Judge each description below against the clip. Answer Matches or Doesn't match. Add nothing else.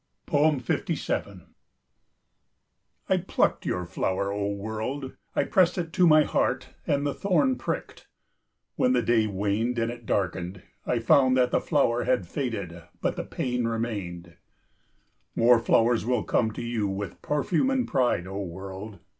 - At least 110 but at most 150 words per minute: Matches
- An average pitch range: Matches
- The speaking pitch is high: Doesn't match